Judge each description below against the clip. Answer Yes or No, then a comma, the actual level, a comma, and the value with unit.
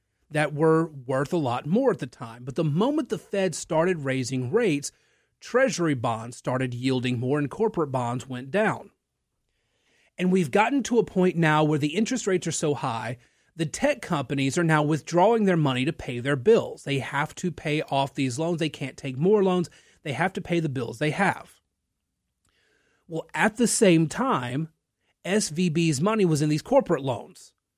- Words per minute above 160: Yes, average, 185 wpm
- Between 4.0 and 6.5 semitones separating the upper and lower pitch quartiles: Yes, average, 5.3 semitones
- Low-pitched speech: No, medium, 160 Hz